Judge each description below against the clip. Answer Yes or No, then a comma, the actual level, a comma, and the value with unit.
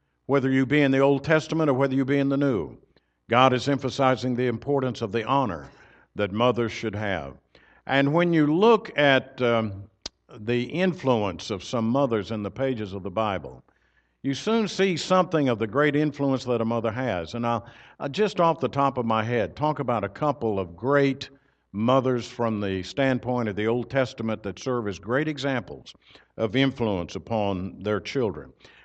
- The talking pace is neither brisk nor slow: Yes, average, 185 wpm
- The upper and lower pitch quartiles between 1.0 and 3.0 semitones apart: No, average, 3.9 semitones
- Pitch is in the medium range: No, low, 125 Hz